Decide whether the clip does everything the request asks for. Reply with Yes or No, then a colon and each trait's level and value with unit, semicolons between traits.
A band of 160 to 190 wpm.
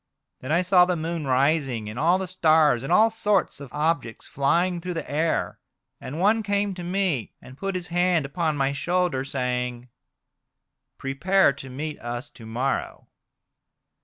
Yes: average, 165 wpm